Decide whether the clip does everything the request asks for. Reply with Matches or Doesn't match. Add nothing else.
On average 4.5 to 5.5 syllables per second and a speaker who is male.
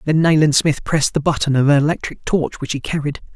Doesn't match